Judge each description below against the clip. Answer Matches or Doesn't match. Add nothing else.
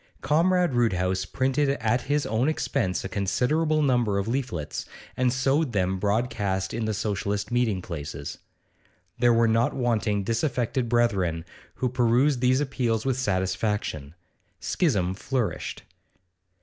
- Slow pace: Matches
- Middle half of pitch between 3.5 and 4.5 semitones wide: Doesn't match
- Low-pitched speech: Matches